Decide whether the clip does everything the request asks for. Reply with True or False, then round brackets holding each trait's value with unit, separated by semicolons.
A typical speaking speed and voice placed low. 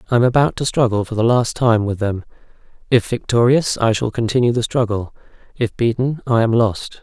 True (195 wpm; 115 Hz)